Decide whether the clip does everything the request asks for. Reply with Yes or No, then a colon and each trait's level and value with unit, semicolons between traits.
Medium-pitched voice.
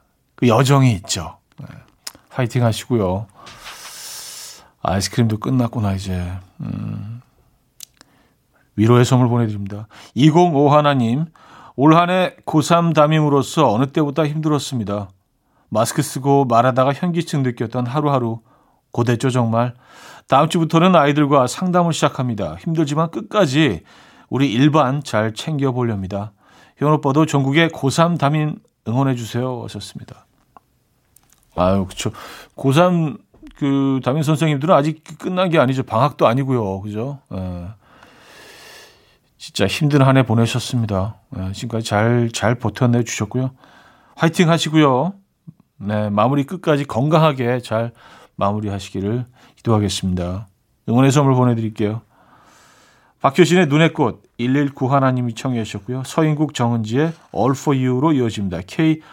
No: low, 130 Hz